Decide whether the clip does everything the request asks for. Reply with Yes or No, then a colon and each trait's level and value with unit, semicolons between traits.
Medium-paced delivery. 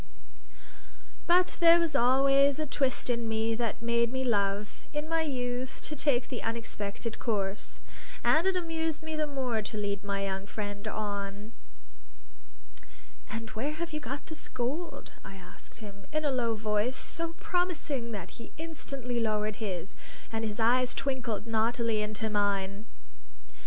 Yes: average, 150 wpm